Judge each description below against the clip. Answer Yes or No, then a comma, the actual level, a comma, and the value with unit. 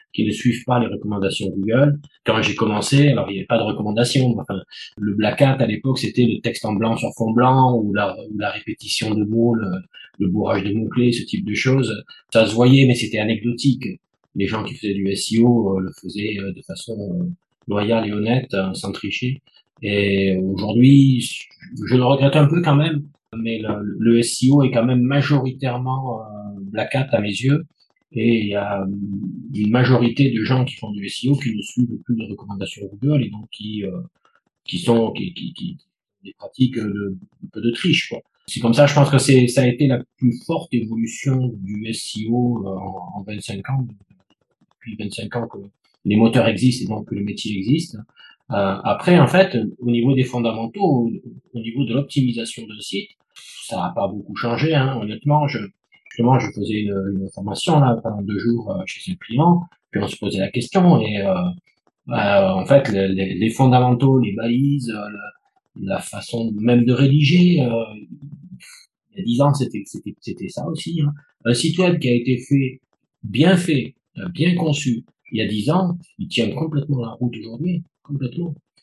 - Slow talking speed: No, average, 195 wpm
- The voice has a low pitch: Yes, low, 120 Hz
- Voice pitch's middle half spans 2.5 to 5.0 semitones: Yes, average, 4.6 semitones